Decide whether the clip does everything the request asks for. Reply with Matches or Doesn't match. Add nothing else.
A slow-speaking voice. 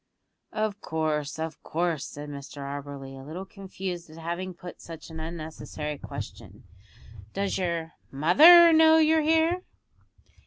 Matches